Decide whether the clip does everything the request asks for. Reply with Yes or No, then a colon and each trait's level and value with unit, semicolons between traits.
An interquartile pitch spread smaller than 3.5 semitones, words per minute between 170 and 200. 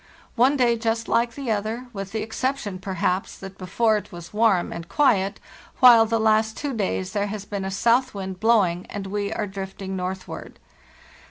Yes: average, 3.1 semitones; average, 180 wpm